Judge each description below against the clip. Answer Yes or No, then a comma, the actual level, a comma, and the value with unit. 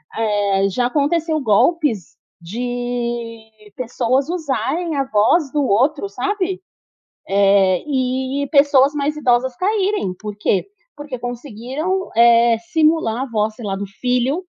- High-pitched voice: Yes, very high, 250 Hz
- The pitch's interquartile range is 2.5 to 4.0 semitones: No, average, 5.2 semitones